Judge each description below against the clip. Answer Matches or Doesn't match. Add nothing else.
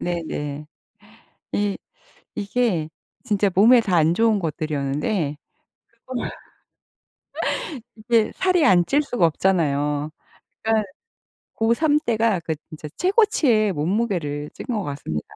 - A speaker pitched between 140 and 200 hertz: Matches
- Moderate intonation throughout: Doesn't match